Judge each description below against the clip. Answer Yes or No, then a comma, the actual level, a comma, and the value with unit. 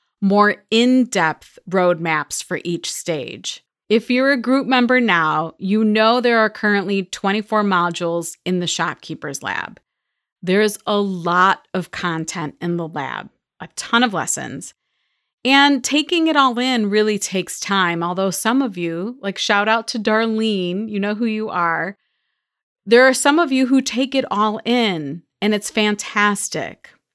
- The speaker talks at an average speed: Yes, average, 155 wpm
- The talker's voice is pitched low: No, high, 210 Hz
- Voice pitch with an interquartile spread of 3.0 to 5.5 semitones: Yes, average, 5.2 semitones